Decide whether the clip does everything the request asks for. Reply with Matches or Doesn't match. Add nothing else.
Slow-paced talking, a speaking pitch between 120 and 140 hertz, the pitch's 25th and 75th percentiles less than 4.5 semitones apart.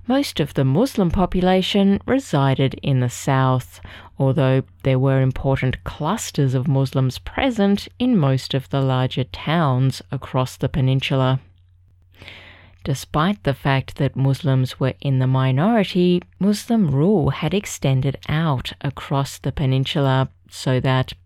Matches